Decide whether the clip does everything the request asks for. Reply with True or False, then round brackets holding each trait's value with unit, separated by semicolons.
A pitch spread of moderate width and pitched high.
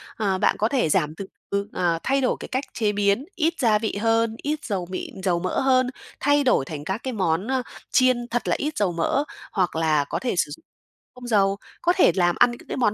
False (5.7 semitones; 215 Hz)